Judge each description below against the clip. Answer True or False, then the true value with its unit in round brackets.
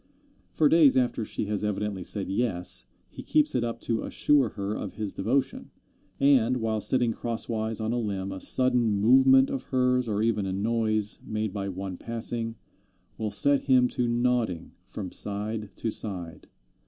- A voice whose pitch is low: True (110 Hz)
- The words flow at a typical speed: True (165 wpm)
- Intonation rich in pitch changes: False (3.3 semitones)